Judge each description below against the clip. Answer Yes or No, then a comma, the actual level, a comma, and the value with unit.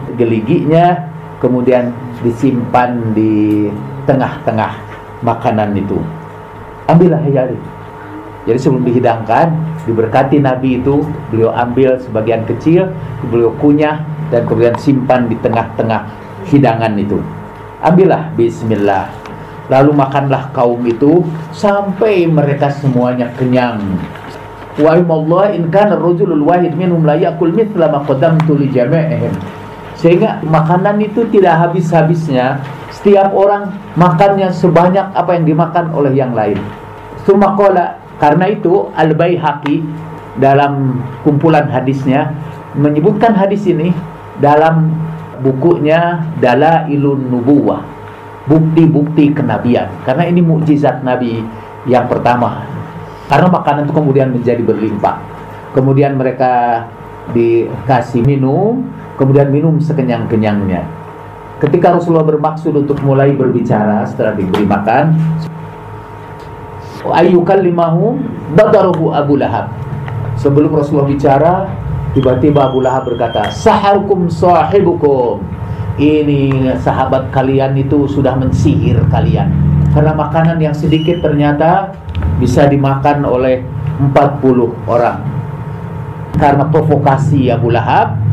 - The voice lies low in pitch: No, medium, 145 Hz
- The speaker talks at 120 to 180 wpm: No, average, 95 wpm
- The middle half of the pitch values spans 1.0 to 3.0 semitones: No, average, 4.7 semitones